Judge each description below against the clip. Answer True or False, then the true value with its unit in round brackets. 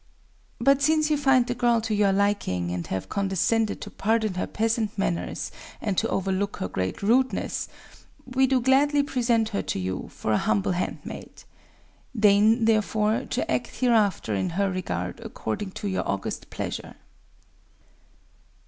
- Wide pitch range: False (4.7 semitones)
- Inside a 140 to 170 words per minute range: True (150 wpm)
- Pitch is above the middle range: True (210 Hz)